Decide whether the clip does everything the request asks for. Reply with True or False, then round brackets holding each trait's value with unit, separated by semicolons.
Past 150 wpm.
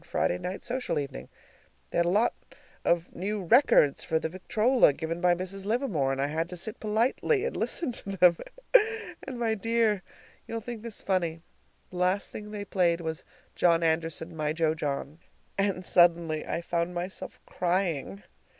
True (170 wpm)